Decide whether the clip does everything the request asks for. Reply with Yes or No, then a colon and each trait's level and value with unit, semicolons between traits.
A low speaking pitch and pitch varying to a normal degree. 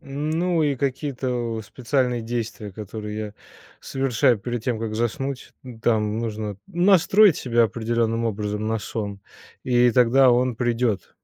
Yes: low, 120 Hz; average, 3.0 semitones